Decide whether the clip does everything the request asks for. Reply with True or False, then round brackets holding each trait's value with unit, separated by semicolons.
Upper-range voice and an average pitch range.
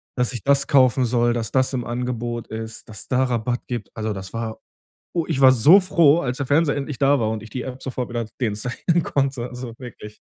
False (125 Hz; 3.0 semitones)